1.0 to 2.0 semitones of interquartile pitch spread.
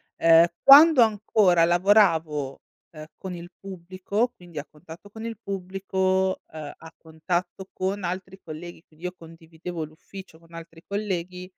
No: average, 2.8 semitones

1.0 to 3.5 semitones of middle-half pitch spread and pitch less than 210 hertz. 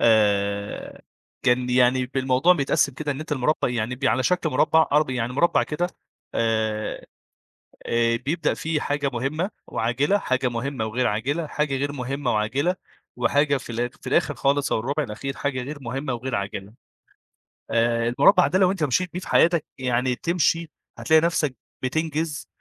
No: average, 4.1 semitones; low, 135 Hz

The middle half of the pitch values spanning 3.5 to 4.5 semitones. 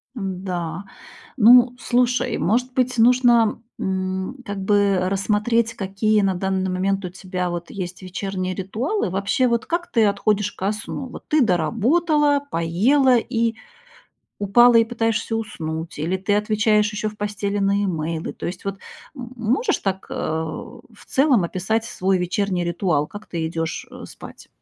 Yes: average, 4.0 semitones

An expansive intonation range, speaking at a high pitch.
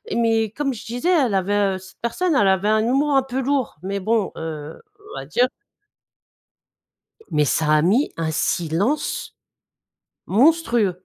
Yes: wide, 6.2 semitones; high, 215 Hz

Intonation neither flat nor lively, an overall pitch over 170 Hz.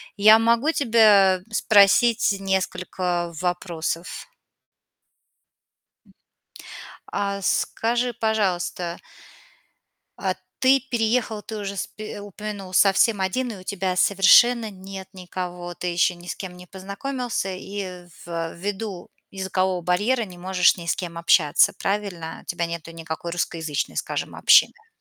Yes: average, 3.3 semitones; high, 190 Hz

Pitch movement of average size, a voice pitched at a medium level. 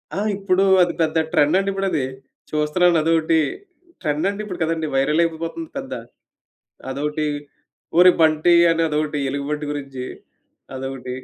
Yes: average, 3.0 semitones; medium, 160 Hz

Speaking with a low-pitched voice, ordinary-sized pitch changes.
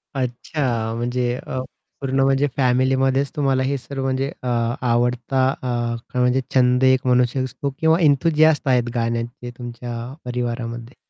No: low, 130 Hz; narrow, 1.8 semitones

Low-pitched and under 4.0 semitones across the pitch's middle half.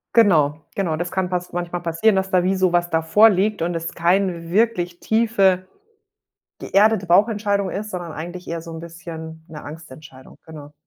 No: medium, 175 Hz; average, 2.9 semitones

